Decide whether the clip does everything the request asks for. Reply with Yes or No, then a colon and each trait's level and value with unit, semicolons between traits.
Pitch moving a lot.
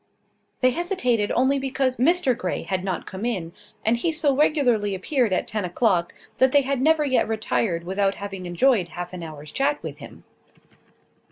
Yes: wide, 6.3 semitones